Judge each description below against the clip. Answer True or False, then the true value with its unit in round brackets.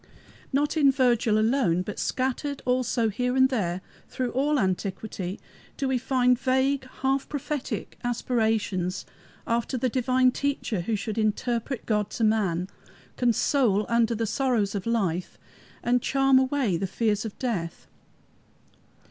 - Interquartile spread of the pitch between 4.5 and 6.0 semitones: False (3.8 semitones)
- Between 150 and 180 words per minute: False (135 wpm)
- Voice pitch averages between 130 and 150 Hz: False (235 Hz)